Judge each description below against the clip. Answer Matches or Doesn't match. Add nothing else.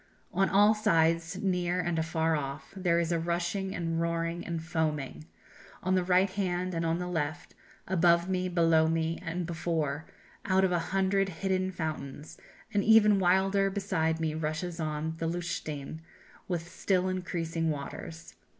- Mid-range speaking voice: Matches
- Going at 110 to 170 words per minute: Matches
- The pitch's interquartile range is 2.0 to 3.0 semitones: Matches